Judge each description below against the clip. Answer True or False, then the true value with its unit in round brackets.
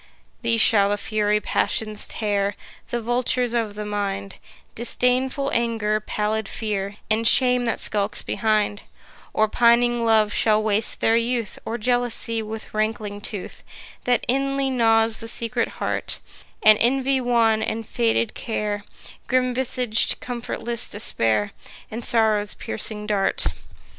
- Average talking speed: False (130 wpm)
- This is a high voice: True (225 Hz)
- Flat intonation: True (2.3 semitones)